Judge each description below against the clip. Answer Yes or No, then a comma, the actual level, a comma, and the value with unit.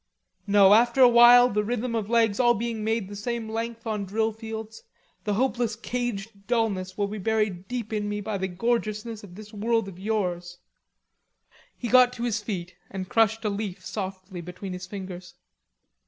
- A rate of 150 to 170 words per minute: No, average, 180 wpm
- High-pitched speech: Yes, high, 215 Hz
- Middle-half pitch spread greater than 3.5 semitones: No, average, 2.8 semitones